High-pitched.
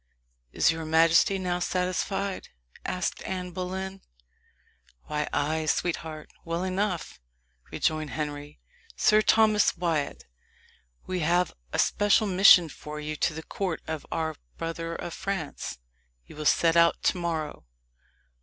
No: medium, 170 Hz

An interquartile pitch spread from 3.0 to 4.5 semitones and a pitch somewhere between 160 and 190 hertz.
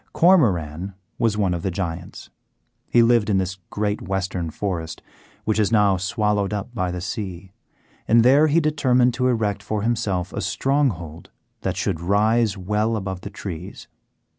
No: average, 4.1 semitones; low, 105 Hz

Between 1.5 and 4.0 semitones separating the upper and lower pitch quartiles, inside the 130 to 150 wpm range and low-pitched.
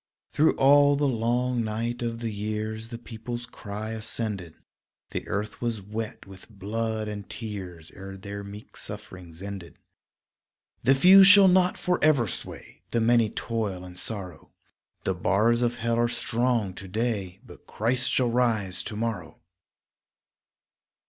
Yes: average, 3.1 semitones; average, 140 wpm; low, 110 Hz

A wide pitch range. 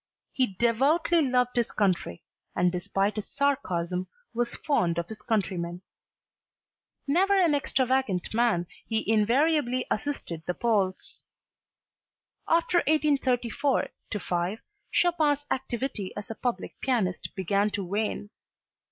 Yes: wide, 6.6 semitones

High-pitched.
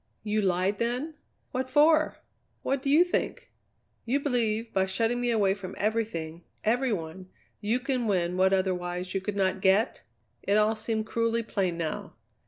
Yes: high, 215 Hz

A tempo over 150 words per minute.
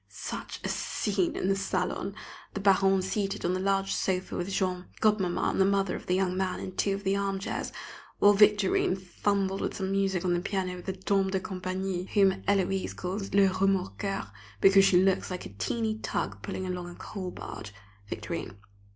Yes: average, 190 wpm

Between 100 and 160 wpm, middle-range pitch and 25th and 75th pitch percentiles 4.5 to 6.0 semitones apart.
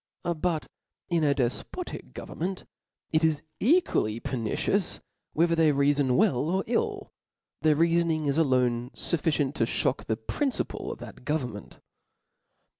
Yes: average, 150 wpm; medium, 155 Hz; average, 4.8 semitones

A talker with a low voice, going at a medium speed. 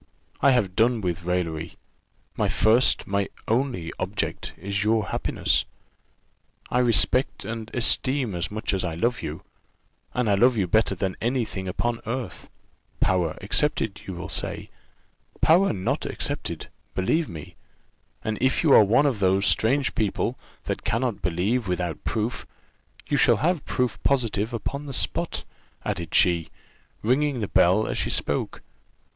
Yes: low, 110 Hz; average, 150 wpm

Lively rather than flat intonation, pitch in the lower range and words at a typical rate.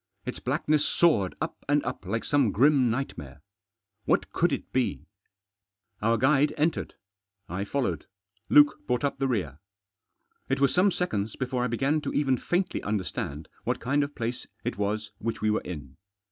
Yes: wide, 5.8 semitones; low, 125 Hz; average, 165 wpm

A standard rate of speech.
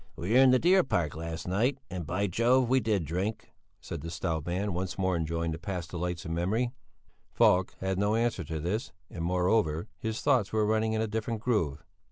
No: fast, 210 wpm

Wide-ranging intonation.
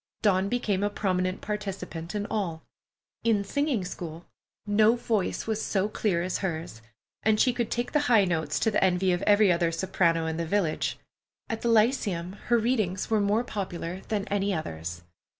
No: average, 3.7 semitones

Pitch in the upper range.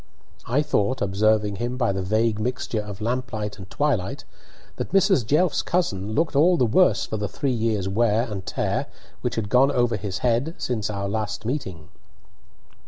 No: low, 115 Hz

